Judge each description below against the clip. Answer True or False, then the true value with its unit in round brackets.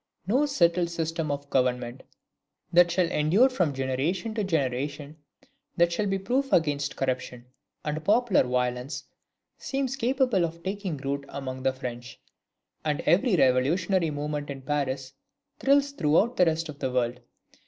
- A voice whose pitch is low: False (155 Hz)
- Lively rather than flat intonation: True (6.1 semitones)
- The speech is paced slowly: False (145 wpm)